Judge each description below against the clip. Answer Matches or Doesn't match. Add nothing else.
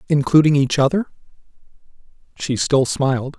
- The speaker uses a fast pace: Doesn't match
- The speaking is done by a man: Matches